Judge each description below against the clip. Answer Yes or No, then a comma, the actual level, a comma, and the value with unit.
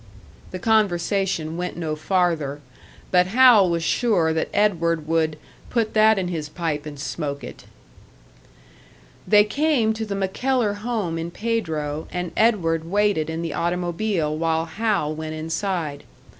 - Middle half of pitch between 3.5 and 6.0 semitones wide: Yes, average, 4.6 semitones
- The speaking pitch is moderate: Yes, medium, 175 Hz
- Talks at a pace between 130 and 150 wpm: Yes, average, 140 wpm